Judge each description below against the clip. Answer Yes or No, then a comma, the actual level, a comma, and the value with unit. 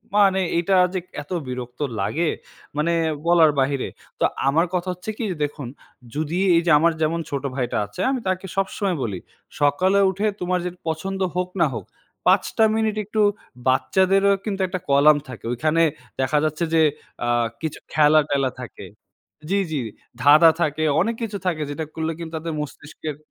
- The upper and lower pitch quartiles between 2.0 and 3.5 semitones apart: No, average, 4.3 semitones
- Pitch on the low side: No, medium, 160 Hz